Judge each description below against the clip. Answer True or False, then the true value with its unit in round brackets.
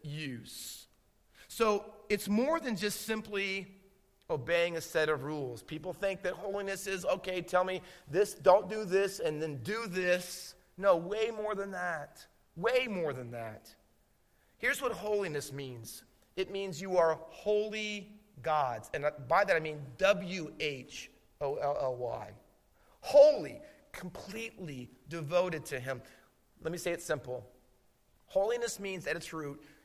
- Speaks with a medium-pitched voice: True (180 Hz)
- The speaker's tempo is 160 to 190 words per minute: False (145 wpm)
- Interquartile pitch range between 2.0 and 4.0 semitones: False (5.3 semitones)